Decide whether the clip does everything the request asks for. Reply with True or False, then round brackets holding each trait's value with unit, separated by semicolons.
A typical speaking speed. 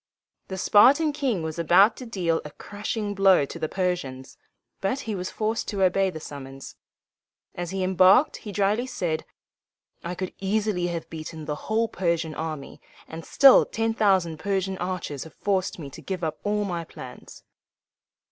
True (165 wpm)